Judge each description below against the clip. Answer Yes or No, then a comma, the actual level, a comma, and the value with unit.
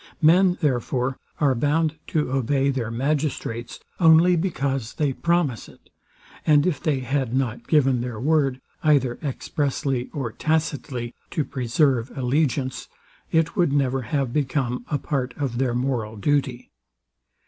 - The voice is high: No, low, 135 Hz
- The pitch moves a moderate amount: Yes, average, 3.4 semitones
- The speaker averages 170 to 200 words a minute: No, slow, 135 wpm